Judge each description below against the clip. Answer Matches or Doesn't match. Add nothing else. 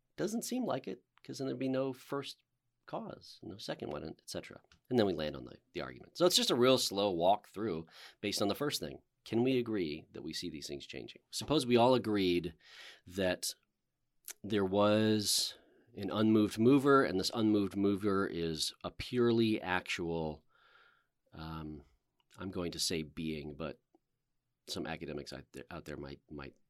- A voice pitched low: Matches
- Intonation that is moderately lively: Doesn't match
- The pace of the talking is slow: Doesn't match